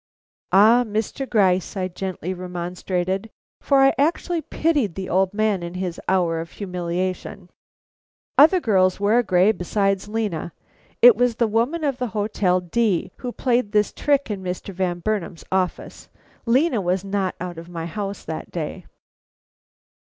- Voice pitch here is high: Yes, high, 195 Hz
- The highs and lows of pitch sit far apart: No, average, 4.0 semitones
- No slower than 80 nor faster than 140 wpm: No, average, 150 wpm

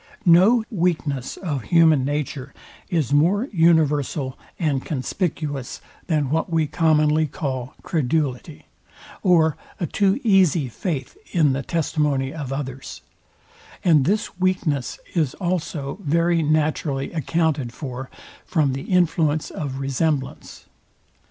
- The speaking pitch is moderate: Yes, medium, 155 Hz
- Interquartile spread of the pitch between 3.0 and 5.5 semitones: Yes, average, 3.5 semitones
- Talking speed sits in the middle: No, slow, 115 wpm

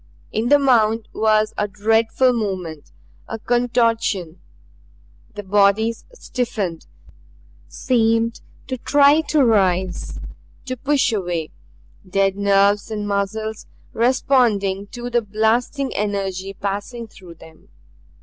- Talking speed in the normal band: No, slow, 105 wpm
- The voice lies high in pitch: Yes, high, 215 Hz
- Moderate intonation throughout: Yes, average, 3.3 semitones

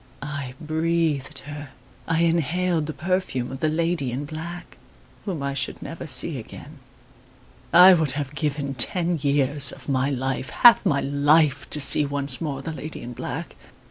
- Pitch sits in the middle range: Yes, medium, 145 Hz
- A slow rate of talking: No, average, 165 wpm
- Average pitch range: Yes, average, 3.0 semitones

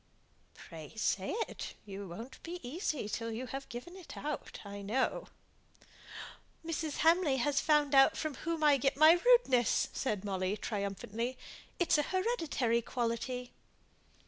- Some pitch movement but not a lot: No, wide, 5.8 semitones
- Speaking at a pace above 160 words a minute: No, average, 140 wpm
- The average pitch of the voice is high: Yes, very high, 260 Hz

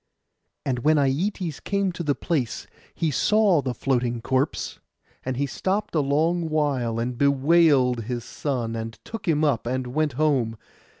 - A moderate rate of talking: Yes, average, 160 wpm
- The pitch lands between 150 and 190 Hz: No, medium, 140 Hz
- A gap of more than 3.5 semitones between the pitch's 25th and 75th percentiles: Yes, average, 4.6 semitones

